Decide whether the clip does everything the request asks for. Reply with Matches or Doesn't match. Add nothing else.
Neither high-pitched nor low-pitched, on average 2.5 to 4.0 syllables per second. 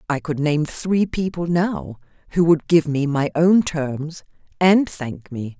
Matches